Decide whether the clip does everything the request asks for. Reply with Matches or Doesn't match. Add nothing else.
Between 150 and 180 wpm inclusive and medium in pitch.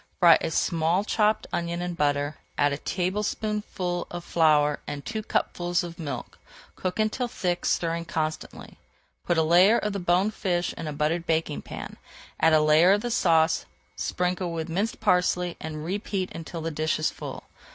Matches